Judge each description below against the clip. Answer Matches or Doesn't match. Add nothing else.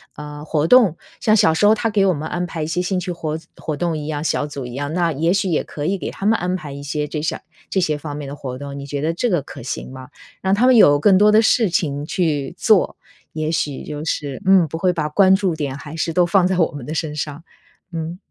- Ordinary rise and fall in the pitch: Matches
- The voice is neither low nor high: Matches